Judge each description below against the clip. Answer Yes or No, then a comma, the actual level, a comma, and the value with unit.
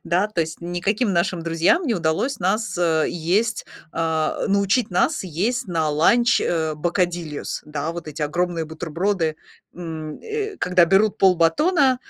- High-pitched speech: No, medium, 175 Hz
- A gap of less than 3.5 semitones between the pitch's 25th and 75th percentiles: No, average, 4.3 semitones